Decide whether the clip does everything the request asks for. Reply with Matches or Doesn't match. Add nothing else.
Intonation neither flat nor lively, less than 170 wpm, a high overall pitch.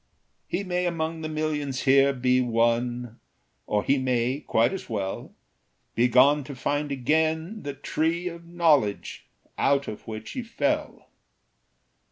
Doesn't match